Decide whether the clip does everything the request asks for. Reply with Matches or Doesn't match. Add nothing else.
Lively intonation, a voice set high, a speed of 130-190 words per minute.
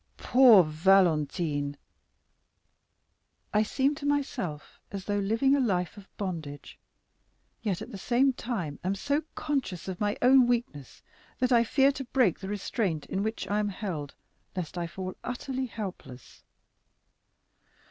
Matches